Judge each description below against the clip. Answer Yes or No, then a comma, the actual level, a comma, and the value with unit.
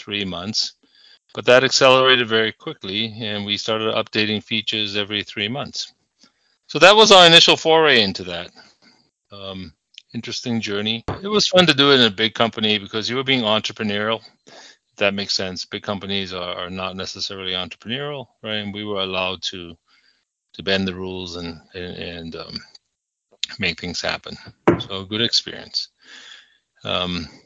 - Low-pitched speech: Yes, low, 105 Hz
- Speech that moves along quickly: No, average, 160 wpm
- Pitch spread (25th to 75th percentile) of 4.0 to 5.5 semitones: No, average, 3.6 semitones